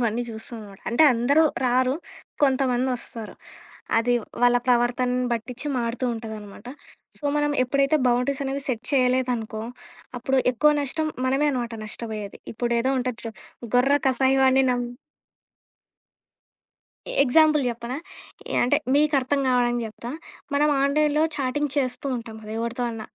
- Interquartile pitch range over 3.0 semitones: No, average, 2.7 semitones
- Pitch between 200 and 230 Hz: No, very high, 250 Hz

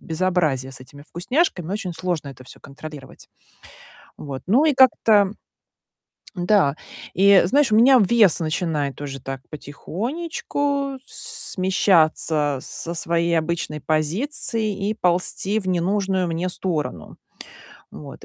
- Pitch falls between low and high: Yes, medium, 175 Hz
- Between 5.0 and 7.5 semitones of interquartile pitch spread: Yes, wide, 5.5 semitones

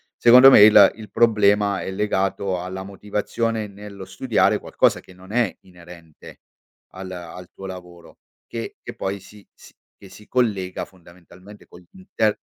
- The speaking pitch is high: No, low, 100 Hz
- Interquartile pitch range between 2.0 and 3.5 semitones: Yes, narrow, 2.4 semitones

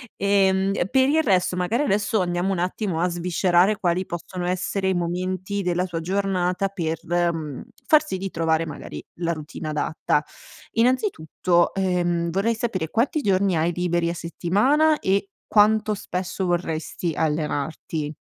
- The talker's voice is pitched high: No, medium, 180 Hz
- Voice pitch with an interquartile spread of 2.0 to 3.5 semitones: Yes, average, 2.7 semitones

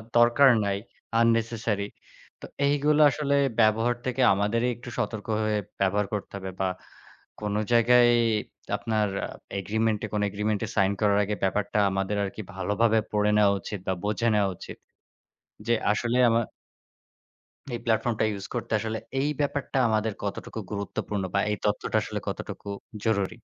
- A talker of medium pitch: No, low, 110 Hz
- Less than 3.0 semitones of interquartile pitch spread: Yes, narrow, 2.4 semitones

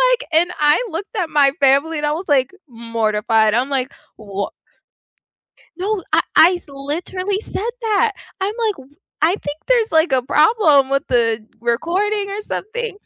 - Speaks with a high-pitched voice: Yes, very high, 315 Hz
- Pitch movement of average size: No, wide, 7.2 semitones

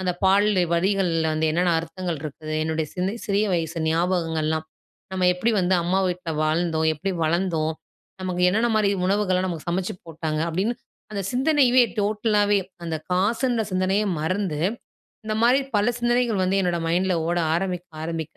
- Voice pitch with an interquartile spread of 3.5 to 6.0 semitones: Yes, average, 3.9 semitones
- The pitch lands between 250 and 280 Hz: No, medium, 185 Hz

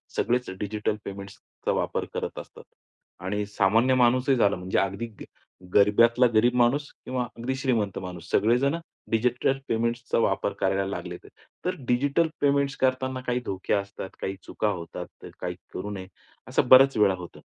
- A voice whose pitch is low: Yes, low, 115 Hz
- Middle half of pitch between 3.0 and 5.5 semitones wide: Yes, average, 4.4 semitones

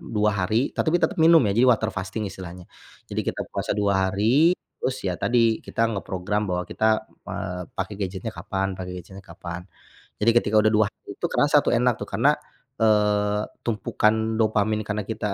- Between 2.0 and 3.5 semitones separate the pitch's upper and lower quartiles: Yes, average, 2.7 semitones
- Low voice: Yes, low, 105 Hz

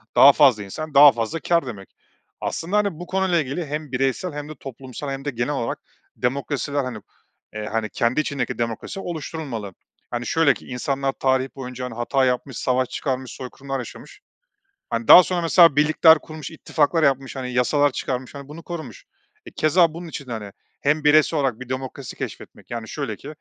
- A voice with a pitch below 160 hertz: Yes, low, 135 Hz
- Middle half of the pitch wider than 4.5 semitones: No, average, 3.7 semitones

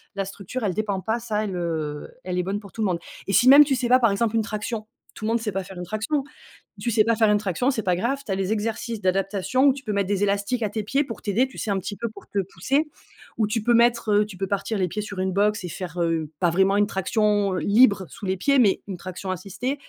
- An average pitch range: Yes, average, 3.2 semitones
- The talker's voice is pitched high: Yes, high, 205 Hz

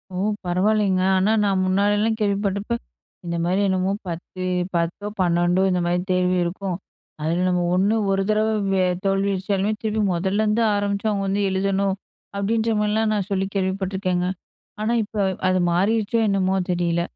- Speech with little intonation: Yes, narrow, 2.1 semitones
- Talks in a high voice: Yes, high, 195 Hz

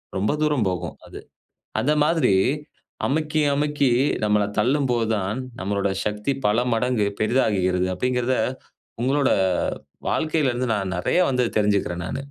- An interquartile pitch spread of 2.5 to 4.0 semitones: No, average, 5.3 semitones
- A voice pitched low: Yes, low, 120 Hz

